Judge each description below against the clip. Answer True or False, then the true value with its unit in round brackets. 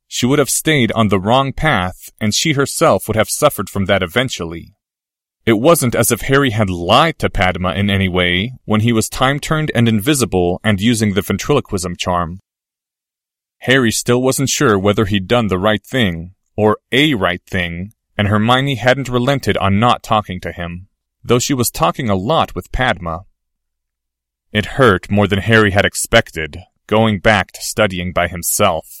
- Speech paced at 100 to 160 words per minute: False (175 wpm)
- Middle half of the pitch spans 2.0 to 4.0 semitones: False (4.9 semitones)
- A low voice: True (105 Hz)